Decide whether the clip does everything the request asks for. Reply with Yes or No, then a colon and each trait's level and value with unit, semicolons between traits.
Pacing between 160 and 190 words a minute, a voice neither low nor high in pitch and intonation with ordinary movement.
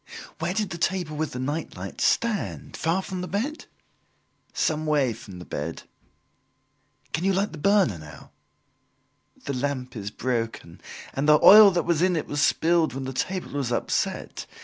No: average, 170 wpm; medium, 150 Hz; wide, 6.5 semitones